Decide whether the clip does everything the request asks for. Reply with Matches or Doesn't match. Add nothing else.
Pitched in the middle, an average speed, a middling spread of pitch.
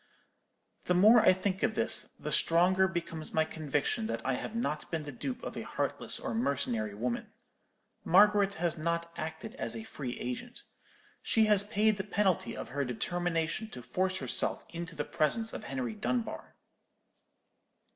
Doesn't match